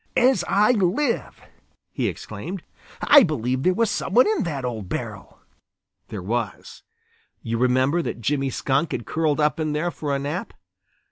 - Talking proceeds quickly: No, average, 160 wpm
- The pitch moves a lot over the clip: Yes, wide, 6.5 semitones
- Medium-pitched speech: Yes, medium, 150 Hz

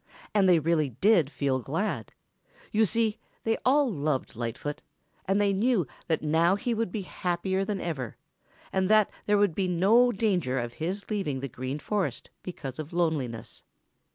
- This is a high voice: No, medium, 180 Hz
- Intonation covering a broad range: Yes, wide, 5.9 semitones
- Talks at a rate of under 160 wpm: No, average, 165 wpm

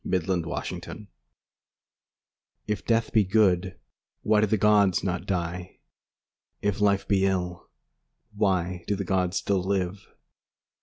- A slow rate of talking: Yes, slow, 115 wpm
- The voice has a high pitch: No, very low, 95 Hz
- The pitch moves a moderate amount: No, narrow, 2.2 semitones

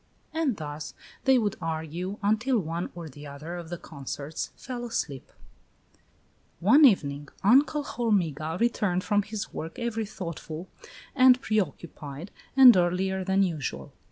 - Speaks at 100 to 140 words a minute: Yes, slow, 135 wpm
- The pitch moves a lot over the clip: Yes, wide, 6.0 semitones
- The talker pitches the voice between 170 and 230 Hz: Yes, medium, 185 Hz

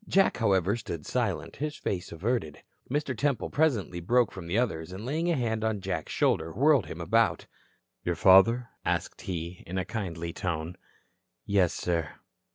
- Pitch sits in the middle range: No, low, 100 Hz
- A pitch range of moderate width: No, wide, 6.0 semitones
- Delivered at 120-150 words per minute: No, average, 160 wpm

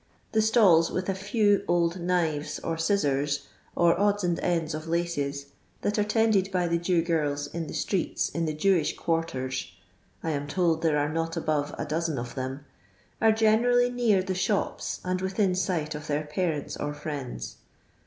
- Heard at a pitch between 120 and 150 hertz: No, medium, 170 Hz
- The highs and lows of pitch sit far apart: No, average, 4.2 semitones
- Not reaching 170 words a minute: No, average, 175 wpm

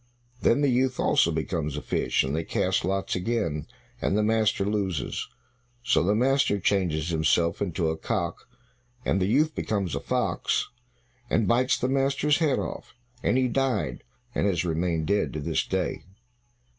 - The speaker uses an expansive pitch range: Yes, wide, 6.7 semitones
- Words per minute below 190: Yes, average, 165 wpm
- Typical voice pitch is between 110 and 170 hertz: No, very low, 95 Hz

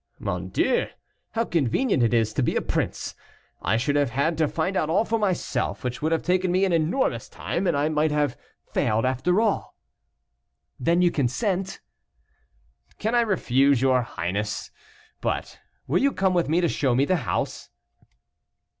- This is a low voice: No, medium, 155 Hz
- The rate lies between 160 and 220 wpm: Yes, average, 170 wpm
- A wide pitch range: Yes, wide, 6.4 semitones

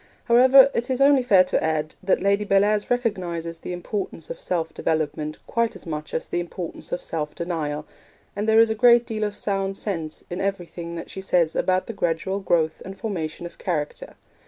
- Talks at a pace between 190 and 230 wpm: Yes, average, 195 wpm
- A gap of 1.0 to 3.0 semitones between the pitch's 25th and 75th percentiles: No, average, 4.5 semitones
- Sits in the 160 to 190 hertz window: Yes, medium, 185 Hz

